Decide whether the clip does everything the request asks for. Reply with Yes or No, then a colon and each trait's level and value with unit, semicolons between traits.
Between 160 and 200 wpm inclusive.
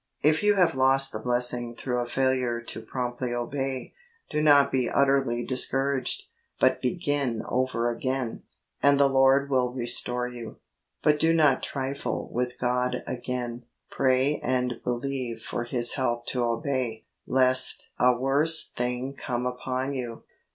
No: average, 145 wpm